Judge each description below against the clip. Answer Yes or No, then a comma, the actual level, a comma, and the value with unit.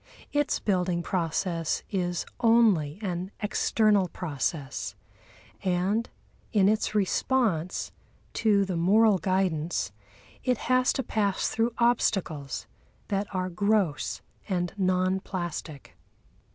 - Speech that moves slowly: Yes, slow, 100 wpm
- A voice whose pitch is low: No, high, 190 Hz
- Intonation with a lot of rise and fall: No, average, 3.7 semitones